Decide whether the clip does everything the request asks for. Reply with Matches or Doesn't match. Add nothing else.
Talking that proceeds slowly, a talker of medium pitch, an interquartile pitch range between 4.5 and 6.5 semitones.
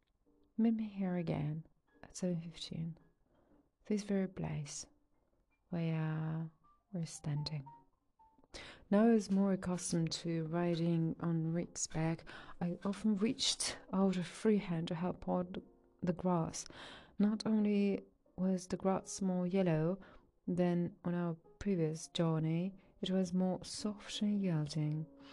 Doesn't match